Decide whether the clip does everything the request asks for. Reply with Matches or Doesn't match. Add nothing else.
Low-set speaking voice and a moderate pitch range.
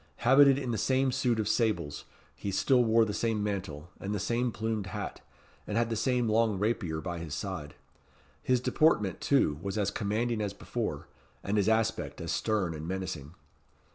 Matches